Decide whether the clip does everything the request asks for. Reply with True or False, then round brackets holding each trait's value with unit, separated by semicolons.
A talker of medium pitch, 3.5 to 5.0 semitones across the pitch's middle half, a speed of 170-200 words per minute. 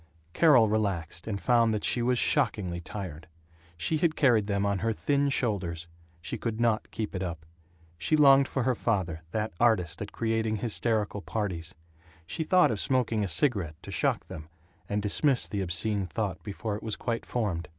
False (105 Hz; 4.2 semitones; 180 wpm)